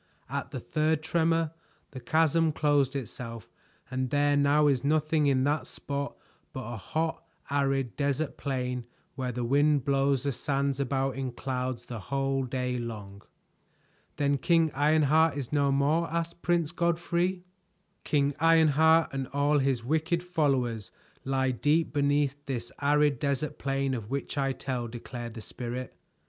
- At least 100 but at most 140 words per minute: No, average, 150 wpm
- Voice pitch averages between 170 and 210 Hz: No, medium, 140 Hz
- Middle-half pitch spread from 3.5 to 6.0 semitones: No, average, 3.0 semitones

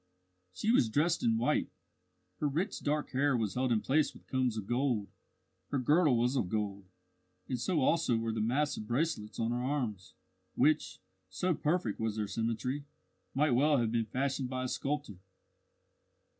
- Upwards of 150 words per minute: Yes, average, 170 wpm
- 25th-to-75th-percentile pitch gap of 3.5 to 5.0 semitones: Yes, average, 4.5 semitones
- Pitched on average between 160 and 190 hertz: No, low, 125 Hz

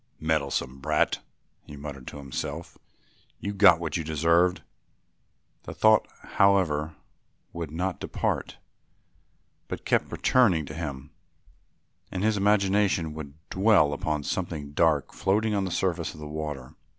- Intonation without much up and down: No, average, 4.5 semitones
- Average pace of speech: No, slow, 130 wpm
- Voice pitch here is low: Yes, very low, 80 Hz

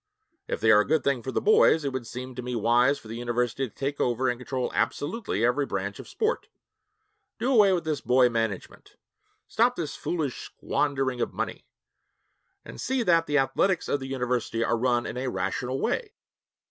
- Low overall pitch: Yes, low, 130 Hz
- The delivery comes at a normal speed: Yes, average, 195 wpm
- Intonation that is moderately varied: Yes, average, 4.6 semitones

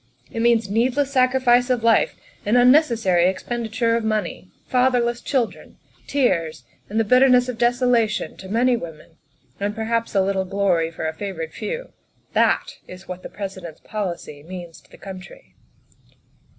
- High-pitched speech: Yes, high, 220 Hz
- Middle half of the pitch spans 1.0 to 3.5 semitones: No, average, 4.7 semitones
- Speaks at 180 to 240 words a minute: No, average, 150 wpm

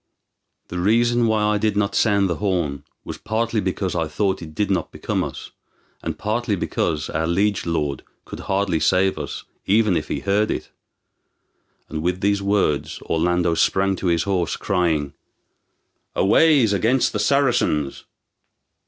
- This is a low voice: Yes, very low, 95 Hz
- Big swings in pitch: No, average, 3.7 semitones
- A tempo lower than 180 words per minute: Yes, average, 155 wpm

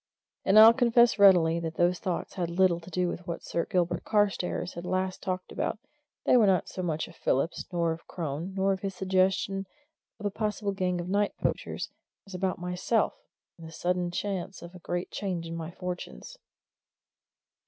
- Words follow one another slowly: No, average, 185 wpm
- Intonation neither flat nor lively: No, narrow, 2.1 semitones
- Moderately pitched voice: Yes, medium, 180 Hz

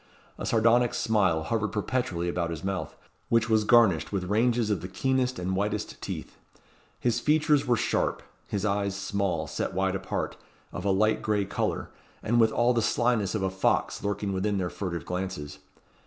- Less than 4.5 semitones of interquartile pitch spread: Yes, average, 3.5 semitones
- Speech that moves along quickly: No, average, 175 wpm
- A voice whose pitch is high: No, low, 105 Hz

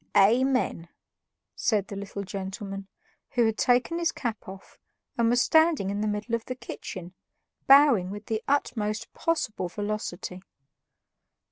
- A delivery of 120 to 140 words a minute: Yes, slow, 135 wpm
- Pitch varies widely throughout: No, average, 3.9 semitones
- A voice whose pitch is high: Yes, high, 215 Hz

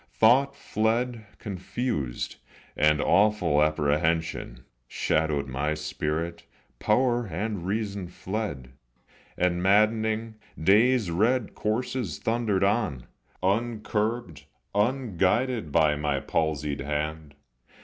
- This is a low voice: Yes, very low, 95 Hz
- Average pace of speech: No, slow, 85 wpm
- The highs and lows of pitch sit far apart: Yes, wide, 6.4 semitones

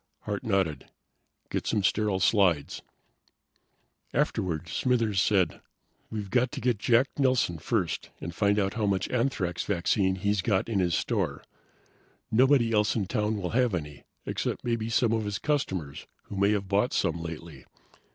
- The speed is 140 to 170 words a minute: Yes, average, 155 wpm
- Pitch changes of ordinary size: Yes, average, 3.9 semitones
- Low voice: Yes, low, 100 Hz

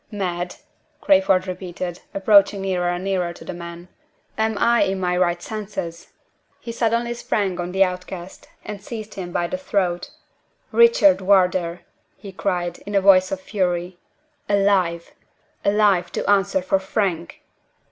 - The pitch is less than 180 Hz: No, high, 190 Hz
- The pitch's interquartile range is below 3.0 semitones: Yes, narrow, 2.5 semitones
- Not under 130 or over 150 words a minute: Yes, average, 145 wpm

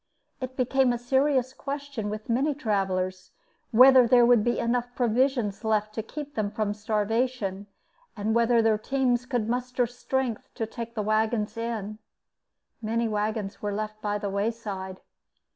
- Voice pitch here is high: Yes, high, 230 Hz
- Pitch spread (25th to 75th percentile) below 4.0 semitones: Yes, average, 2.9 semitones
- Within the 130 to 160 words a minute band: Yes, average, 150 wpm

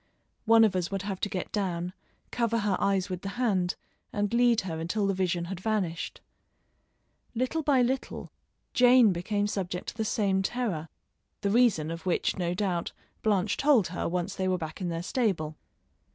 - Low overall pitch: No, high, 195 Hz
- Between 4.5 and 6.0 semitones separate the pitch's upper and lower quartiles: No, average, 3.9 semitones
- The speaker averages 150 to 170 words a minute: No, average, 180 wpm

